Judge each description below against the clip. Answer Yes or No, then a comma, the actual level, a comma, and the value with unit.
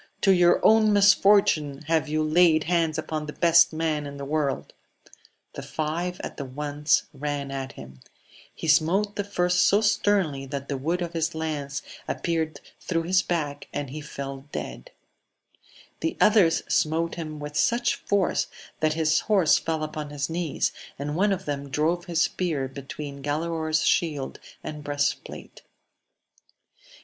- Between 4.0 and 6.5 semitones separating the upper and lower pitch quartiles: No, average, 3.2 semitones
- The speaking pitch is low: No, medium, 155 Hz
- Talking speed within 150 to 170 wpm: Yes, average, 155 wpm